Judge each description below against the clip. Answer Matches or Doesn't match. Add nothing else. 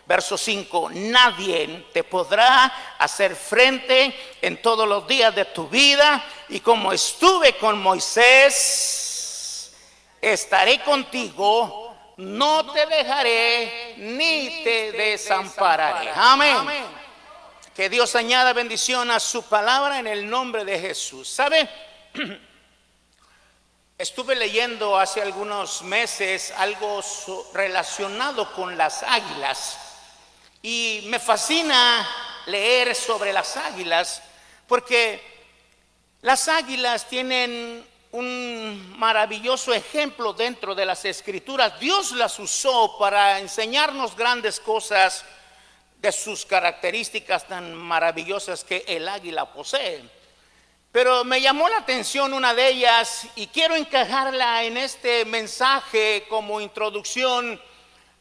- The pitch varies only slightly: Doesn't match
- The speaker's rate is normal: Doesn't match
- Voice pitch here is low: Doesn't match